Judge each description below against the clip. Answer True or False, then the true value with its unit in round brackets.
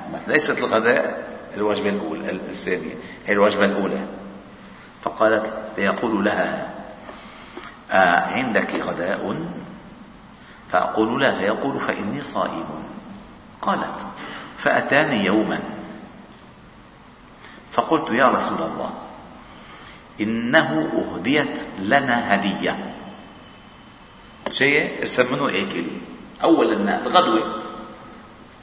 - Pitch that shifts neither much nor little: False (1.6 semitones)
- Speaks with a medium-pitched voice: False (100 Hz)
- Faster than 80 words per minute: False (75 wpm)